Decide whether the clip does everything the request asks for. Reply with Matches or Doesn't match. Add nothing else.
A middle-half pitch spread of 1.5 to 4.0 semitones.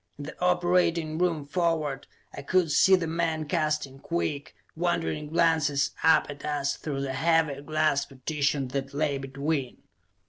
Matches